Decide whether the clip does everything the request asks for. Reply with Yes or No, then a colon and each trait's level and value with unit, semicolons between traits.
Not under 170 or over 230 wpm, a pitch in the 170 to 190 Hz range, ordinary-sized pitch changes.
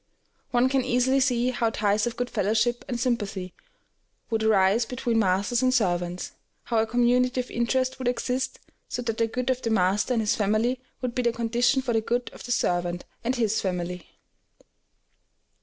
No: average, 180 wpm; high, 235 Hz; average, 3.0 semitones